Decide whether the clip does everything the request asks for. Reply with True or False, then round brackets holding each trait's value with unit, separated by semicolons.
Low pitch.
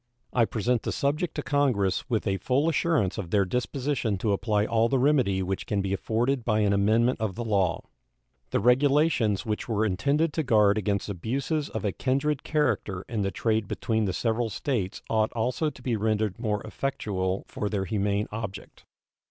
True (110 Hz)